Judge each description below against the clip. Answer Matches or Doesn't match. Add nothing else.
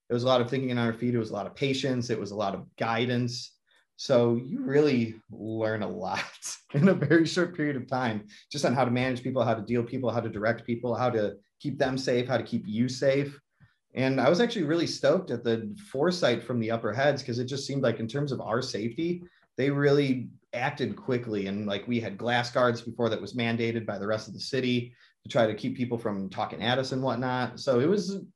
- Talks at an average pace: Doesn't match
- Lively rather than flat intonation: Doesn't match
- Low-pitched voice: Matches